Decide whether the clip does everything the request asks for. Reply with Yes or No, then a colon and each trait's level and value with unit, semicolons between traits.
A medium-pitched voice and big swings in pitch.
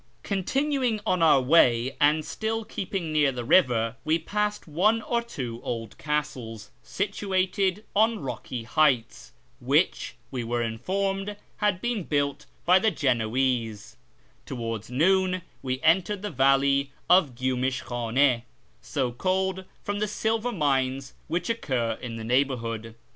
Yes: medium, 145 Hz; wide, 7.5 semitones